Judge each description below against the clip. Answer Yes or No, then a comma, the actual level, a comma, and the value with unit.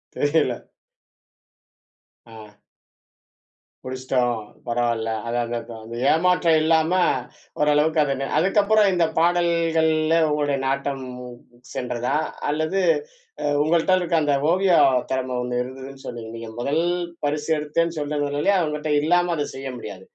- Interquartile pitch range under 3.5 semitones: No, average, 4.1 semitones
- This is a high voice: No, medium, 150 Hz